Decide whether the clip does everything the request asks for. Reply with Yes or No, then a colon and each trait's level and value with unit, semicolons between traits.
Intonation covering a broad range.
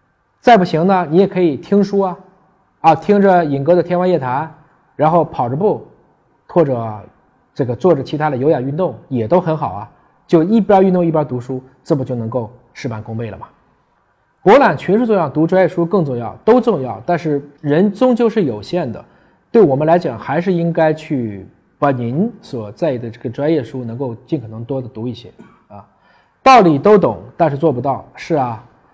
Yes: wide, 6.1 semitones